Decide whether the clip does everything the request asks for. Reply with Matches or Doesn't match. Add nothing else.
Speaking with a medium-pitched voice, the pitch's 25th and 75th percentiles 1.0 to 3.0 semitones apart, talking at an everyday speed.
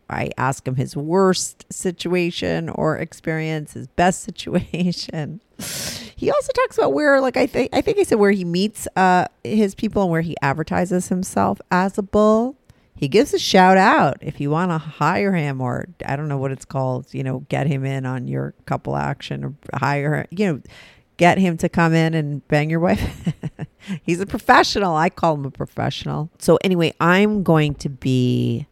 Doesn't match